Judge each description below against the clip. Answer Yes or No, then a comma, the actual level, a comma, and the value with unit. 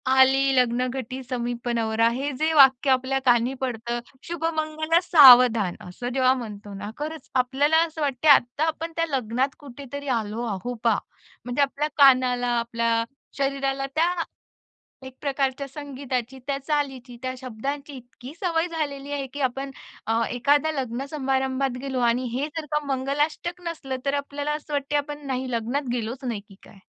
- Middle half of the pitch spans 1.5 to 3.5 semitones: Yes, average, 2.9 semitones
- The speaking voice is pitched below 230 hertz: No, very high, 270 Hz